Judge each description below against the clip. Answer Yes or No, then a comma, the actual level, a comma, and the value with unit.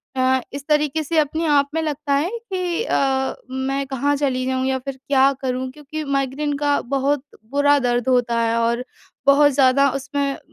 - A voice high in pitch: Yes, very high, 275 Hz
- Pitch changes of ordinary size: No, narrow, 1.9 semitones